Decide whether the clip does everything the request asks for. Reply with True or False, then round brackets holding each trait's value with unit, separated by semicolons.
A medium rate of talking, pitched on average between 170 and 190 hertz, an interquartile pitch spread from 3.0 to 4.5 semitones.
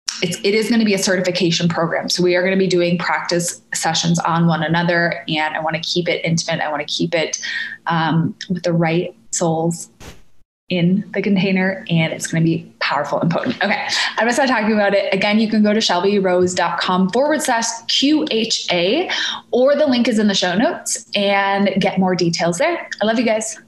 False (210 wpm; 185 Hz; 4.2 semitones)